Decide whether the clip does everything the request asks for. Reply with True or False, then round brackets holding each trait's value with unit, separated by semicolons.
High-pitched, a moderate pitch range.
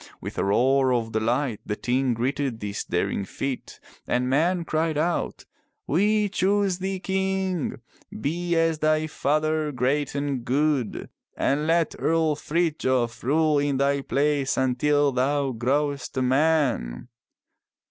False (145 Hz; 3.8 semitones)